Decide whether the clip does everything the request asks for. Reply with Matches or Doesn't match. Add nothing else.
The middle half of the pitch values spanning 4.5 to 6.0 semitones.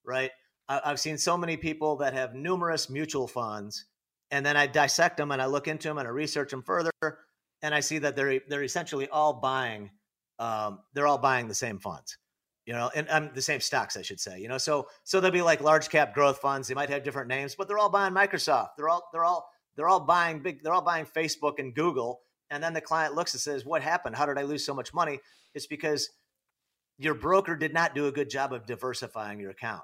Doesn't match